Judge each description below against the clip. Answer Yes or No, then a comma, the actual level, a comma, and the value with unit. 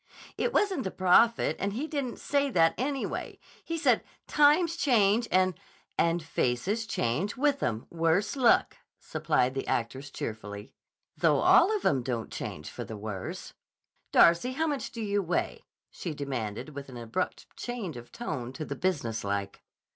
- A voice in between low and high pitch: Yes, medium, 180 Hz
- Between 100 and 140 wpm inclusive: No, average, 160 wpm